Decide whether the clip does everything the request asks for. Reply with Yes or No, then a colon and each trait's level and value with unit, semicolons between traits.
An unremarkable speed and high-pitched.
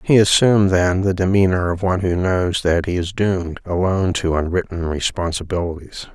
No: average, 165 wpm; very low, 90 Hz